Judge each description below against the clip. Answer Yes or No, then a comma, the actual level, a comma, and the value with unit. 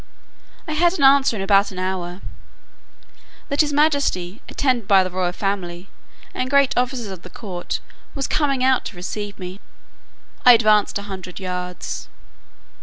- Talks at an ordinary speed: Yes, average, 155 wpm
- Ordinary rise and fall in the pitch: No, wide, 6.3 semitones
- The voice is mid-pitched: No, high, 205 Hz